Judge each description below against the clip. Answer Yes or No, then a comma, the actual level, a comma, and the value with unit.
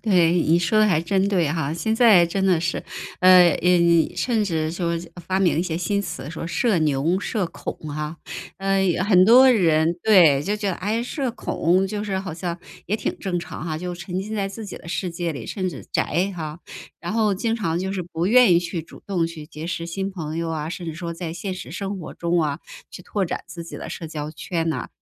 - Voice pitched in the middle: Yes, medium, 175 Hz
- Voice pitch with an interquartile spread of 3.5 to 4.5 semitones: No, average, 3.0 semitones